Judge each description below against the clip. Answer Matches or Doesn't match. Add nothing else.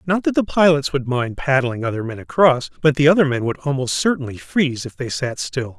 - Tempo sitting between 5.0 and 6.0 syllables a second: Matches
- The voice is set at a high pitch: Doesn't match